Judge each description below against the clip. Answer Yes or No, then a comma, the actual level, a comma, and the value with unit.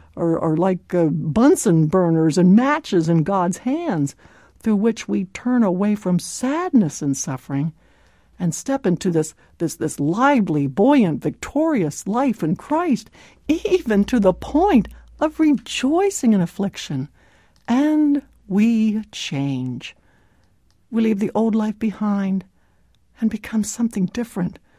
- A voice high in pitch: Yes, high, 200 Hz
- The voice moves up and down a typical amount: No, wide, 6.8 semitones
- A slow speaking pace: Yes, slow, 130 wpm